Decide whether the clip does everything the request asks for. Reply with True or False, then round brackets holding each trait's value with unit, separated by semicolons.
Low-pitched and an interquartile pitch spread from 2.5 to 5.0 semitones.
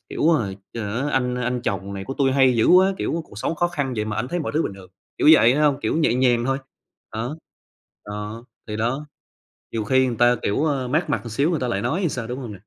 True (125 Hz; 4.5 semitones)